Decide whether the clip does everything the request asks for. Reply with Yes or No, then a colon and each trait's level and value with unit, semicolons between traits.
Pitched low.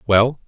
Yes: low, 115 Hz